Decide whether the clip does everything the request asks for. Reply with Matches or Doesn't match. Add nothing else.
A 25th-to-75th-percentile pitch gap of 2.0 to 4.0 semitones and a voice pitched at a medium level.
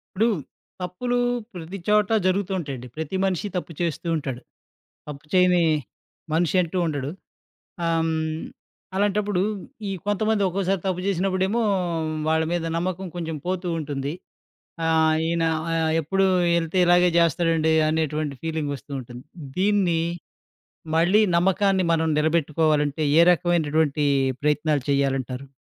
Matches